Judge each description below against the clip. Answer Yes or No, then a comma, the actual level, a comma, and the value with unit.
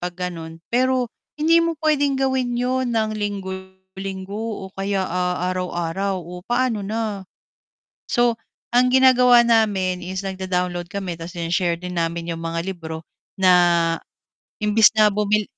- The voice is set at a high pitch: Yes, high, 195 Hz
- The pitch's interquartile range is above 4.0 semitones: Yes, average, 4.8 semitones